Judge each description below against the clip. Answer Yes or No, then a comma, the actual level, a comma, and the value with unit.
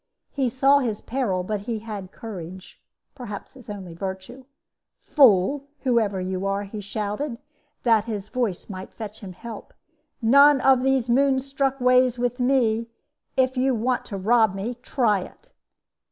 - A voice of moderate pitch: No, high, 230 Hz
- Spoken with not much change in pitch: No, average, 4.4 semitones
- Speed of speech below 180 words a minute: Yes, average, 155 wpm